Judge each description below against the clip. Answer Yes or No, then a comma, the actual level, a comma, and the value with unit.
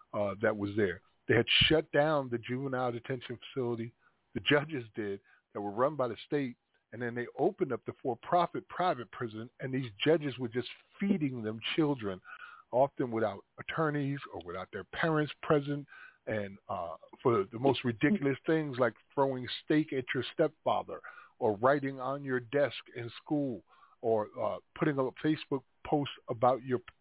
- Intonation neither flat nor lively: Yes, average, 3.5 semitones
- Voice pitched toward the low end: Yes, low, 130 Hz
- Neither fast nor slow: Yes, average, 165 wpm